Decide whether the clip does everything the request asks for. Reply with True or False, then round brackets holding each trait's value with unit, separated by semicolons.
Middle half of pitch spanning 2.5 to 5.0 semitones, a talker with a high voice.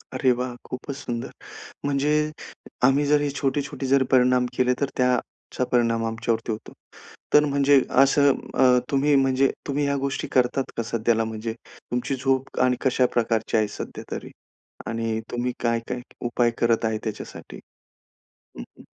False (2.9 semitones; 125 Hz)